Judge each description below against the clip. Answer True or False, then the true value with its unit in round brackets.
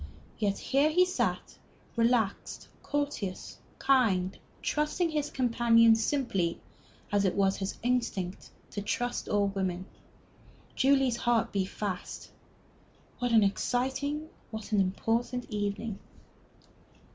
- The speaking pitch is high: True (230 Hz)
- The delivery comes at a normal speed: False (110 wpm)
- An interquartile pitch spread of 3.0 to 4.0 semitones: False (4.8 semitones)